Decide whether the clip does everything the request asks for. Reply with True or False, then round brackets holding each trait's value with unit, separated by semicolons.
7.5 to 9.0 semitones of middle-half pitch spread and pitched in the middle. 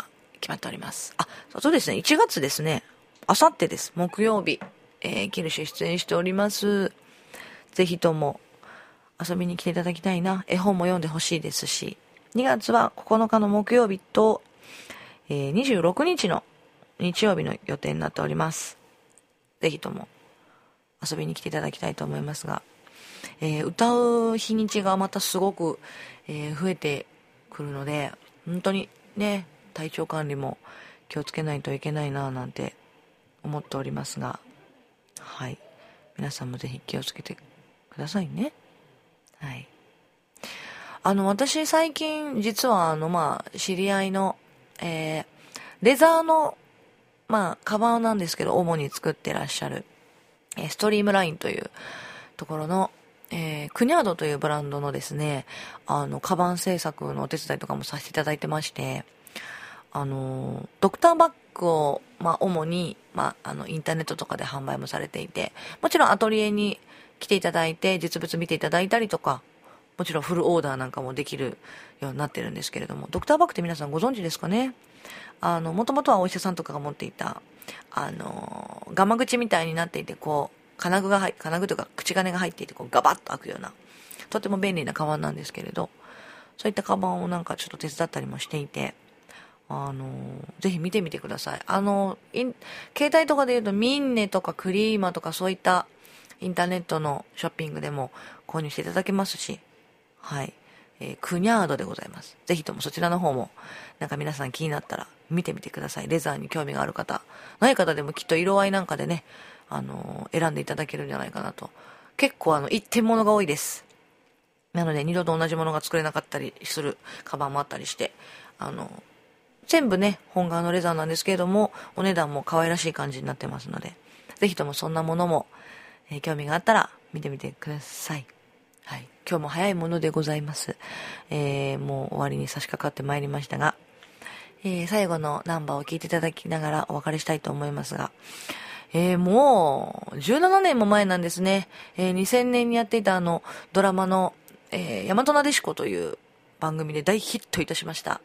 False (5.2 semitones; 175 Hz)